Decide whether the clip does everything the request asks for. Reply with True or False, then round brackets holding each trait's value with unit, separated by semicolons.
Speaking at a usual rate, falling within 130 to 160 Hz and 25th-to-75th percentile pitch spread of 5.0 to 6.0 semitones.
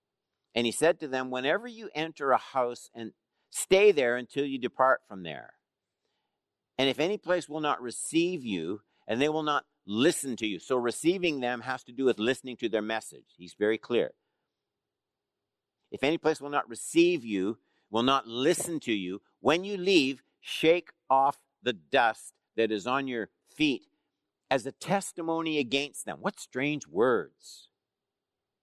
True (165 wpm; 140 Hz; 5.4 semitones)